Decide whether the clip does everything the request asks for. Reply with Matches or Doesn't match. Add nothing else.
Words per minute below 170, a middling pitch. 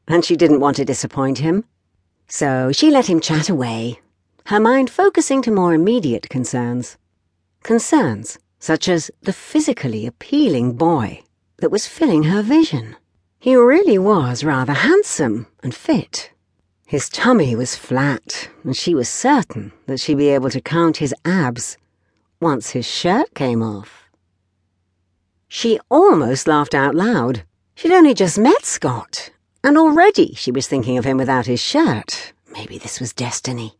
Matches